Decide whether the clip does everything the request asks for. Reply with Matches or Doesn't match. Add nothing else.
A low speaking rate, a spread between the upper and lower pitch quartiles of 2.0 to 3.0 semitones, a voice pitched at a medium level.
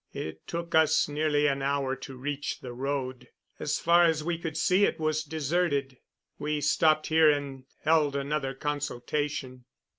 Doesn't match